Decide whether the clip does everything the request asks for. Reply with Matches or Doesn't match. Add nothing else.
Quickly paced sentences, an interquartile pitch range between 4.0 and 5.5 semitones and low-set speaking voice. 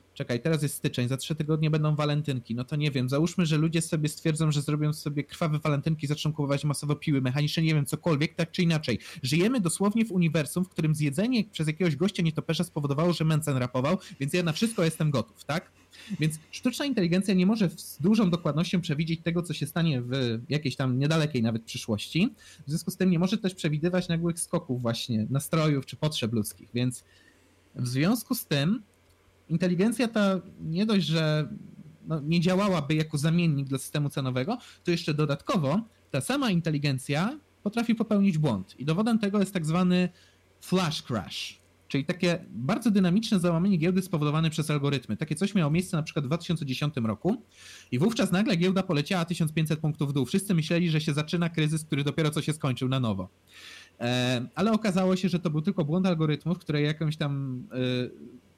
Doesn't match